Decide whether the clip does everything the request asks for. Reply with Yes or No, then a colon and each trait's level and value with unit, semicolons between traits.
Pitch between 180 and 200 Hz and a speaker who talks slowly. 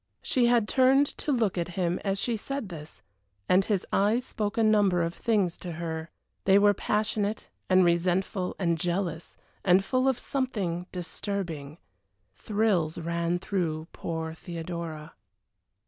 No: medium, 185 Hz; average, 145 wpm